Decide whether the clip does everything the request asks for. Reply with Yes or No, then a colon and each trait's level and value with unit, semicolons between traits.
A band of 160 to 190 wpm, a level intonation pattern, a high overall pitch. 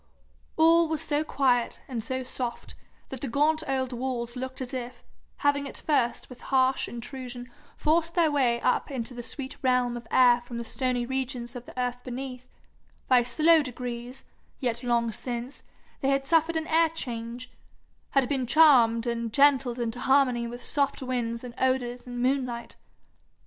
Yes: average, 165 wpm; narrow, 2.3 semitones; very high, 255 Hz